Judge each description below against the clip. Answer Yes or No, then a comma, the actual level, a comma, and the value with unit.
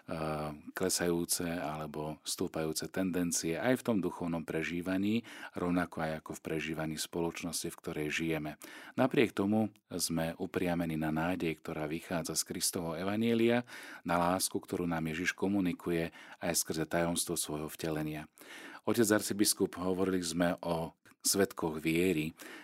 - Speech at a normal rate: Yes, average, 125 wpm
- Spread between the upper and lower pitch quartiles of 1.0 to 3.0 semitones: Yes, average, 2.7 semitones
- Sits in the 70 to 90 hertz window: Yes, very low, 85 Hz